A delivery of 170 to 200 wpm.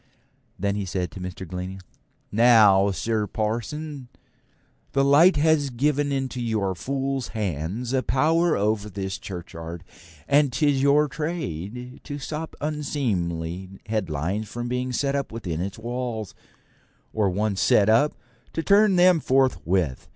No: slow, 135 wpm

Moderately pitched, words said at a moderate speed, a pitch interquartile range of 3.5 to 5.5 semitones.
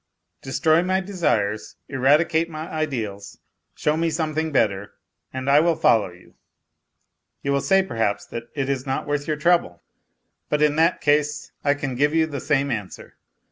Yes: medium, 145 Hz; average, 165 wpm; average, 3.8 semitones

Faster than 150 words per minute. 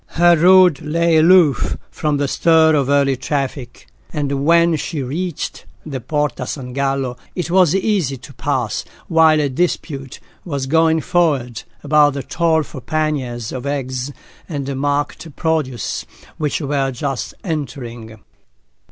No: slow, 135 wpm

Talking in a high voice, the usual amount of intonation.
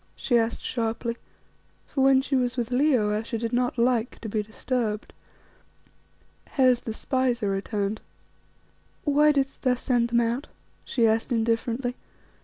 No: high, 240 Hz; narrow, 2.3 semitones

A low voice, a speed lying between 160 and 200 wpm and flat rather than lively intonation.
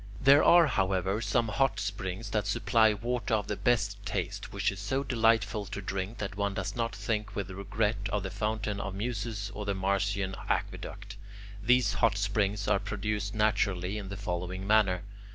Yes: low, 105 Hz; average, 180 wpm; narrow, 2.0 semitones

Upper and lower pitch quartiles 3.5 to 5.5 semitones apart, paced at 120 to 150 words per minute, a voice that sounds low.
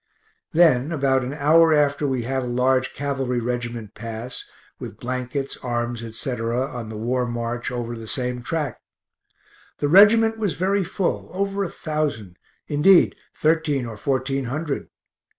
Yes: average, 4.3 semitones; average, 145 wpm; low, 130 Hz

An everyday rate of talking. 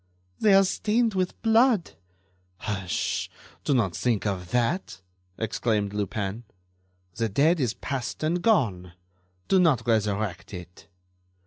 No: slow, 120 wpm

